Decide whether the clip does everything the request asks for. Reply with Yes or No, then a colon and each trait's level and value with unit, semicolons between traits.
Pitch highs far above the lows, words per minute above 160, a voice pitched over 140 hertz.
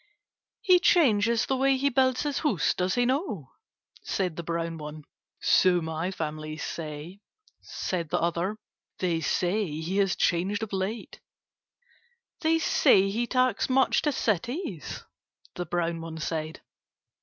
No: wide, 6.9 semitones; average, 140 wpm; high, 190 Hz